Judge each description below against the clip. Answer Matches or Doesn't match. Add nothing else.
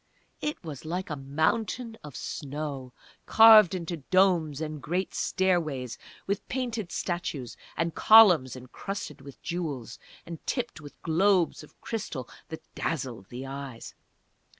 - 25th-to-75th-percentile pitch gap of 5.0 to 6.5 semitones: Matches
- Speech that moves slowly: Matches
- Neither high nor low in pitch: Matches